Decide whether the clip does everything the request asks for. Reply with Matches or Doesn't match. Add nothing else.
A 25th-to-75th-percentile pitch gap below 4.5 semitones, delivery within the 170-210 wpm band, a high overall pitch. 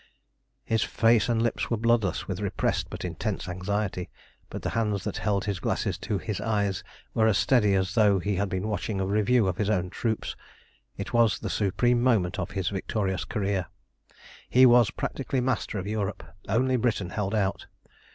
Doesn't match